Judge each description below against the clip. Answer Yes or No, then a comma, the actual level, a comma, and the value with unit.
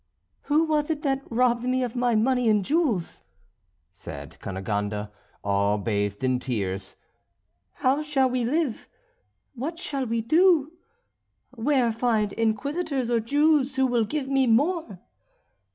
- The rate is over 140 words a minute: No, slow, 135 wpm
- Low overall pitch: No, high, 245 Hz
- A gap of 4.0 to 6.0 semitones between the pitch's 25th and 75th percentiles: Yes, wide, 5.5 semitones